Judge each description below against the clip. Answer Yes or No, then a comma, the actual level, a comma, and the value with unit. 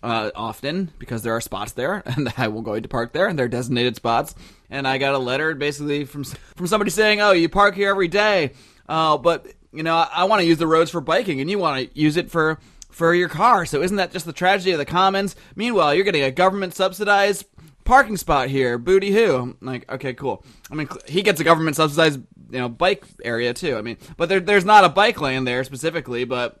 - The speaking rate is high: Yes, fast, 235 wpm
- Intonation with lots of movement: Yes, wide, 6.6 semitones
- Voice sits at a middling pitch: Yes, medium, 160 Hz